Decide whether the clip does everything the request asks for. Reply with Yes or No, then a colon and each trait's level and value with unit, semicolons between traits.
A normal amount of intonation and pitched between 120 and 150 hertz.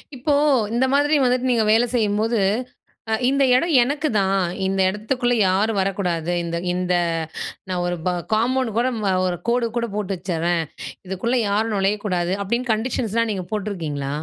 No: average, 4.4 semitones; high, 210 Hz